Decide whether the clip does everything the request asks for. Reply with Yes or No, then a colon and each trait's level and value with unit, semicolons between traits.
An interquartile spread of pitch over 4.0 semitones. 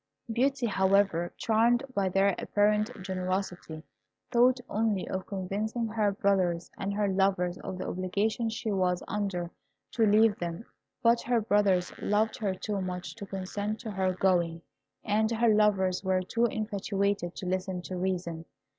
No: average, 2.8 semitones